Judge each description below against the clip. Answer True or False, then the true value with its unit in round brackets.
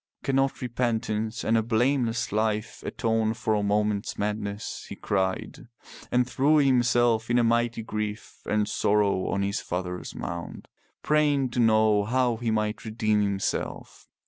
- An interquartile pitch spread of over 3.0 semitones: False (2.4 semitones)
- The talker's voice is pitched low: True (110 Hz)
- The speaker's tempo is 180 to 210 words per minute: False (140 wpm)